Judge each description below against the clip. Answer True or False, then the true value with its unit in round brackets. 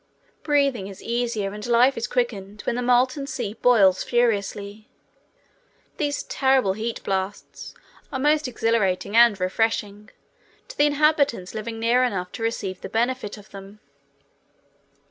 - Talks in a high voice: True (230 Hz)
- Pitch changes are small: False (3.8 semitones)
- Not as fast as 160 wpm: True (135 wpm)